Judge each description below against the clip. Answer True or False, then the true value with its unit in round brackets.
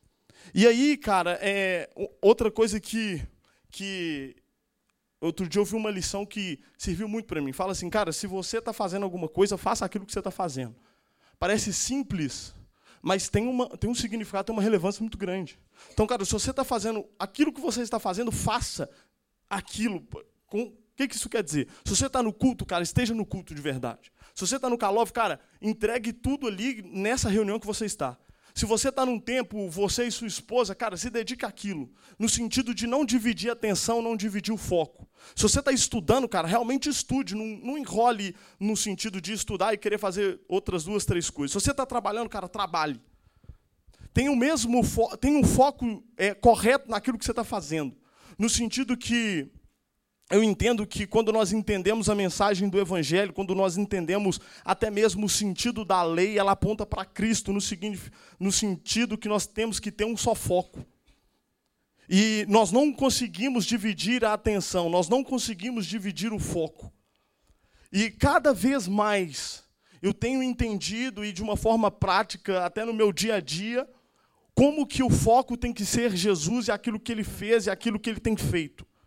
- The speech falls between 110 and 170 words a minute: False (185 wpm)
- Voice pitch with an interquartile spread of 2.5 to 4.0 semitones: True (3.3 semitones)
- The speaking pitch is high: True (215 Hz)